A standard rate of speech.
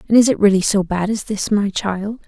No: fast, 265 wpm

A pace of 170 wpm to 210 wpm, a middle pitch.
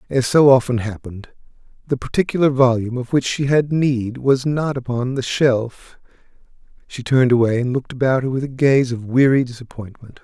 No: average, 175 wpm; low, 130 Hz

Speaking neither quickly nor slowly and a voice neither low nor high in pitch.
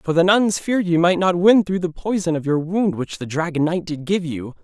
No: fast, 270 wpm; medium, 175 Hz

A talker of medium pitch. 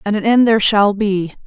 No: high, 205 Hz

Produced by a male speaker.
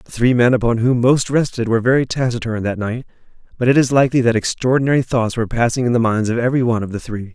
Yes: male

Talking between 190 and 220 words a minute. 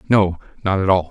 Yes: fast, 215 wpm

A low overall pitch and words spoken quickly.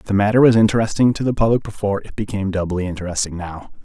Yes: low, 100 Hz; fast, 220 wpm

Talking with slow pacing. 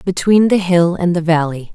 No: fast, 205 wpm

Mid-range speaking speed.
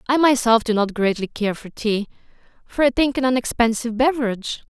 Yes: average, 190 wpm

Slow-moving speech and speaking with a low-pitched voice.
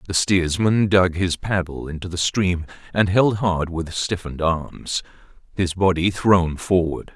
No: average, 150 wpm; very low, 90 Hz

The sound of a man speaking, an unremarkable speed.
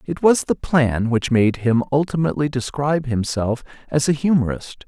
Yes: male; average, 160 wpm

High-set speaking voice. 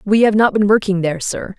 Yes: high, 200 Hz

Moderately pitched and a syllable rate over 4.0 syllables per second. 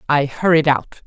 Yes: medium, 145 Hz; 4.5 syllables/s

